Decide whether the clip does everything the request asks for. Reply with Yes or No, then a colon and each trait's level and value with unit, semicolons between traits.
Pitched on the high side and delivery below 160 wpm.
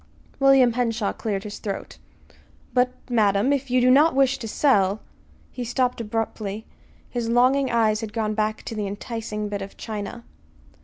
No: high, 225 Hz; average, 165 wpm